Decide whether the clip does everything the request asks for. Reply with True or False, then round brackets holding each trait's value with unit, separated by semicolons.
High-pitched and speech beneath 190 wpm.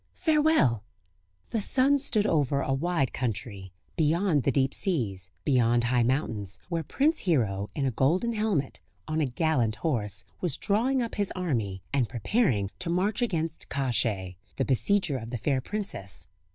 False (140 Hz; 155 wpm)